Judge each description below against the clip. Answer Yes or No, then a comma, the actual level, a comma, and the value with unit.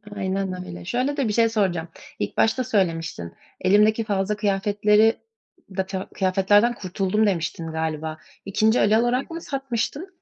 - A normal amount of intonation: Yes, average, 3.4 semitones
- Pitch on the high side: Yes, high, 205 Hz